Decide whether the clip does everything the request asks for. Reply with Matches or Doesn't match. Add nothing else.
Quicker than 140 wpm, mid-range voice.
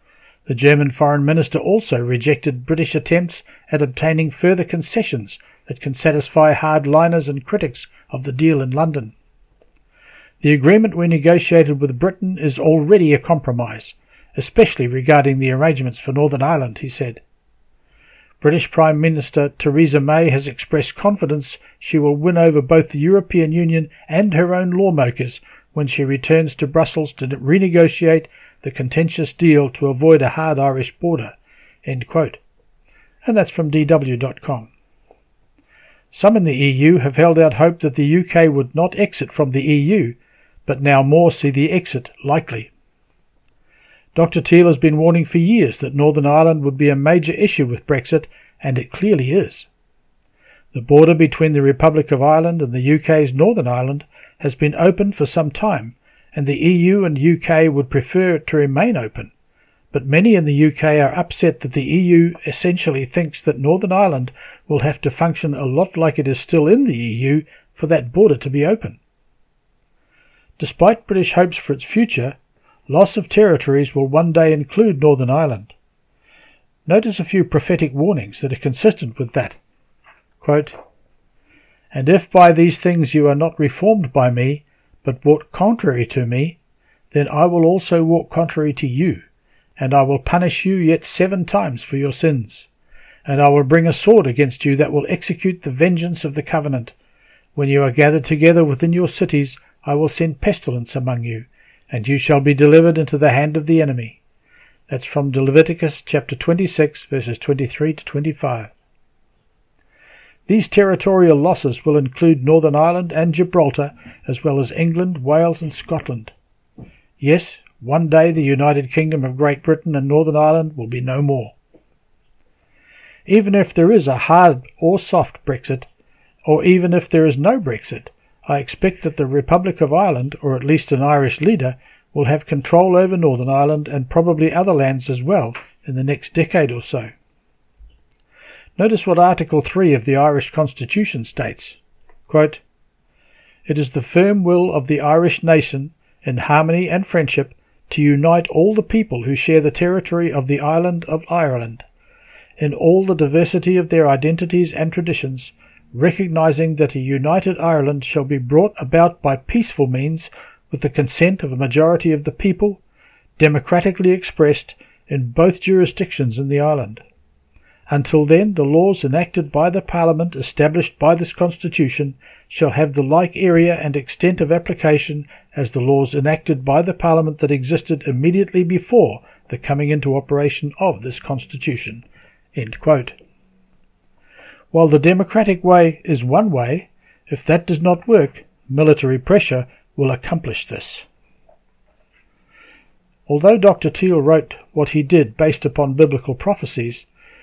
Matches